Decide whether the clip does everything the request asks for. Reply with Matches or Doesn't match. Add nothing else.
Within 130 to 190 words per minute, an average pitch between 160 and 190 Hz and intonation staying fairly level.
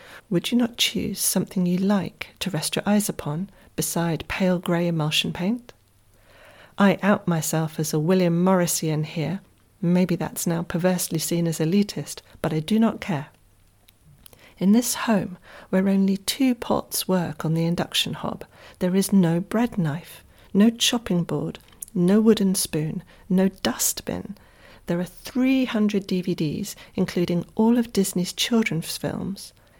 Doesn't match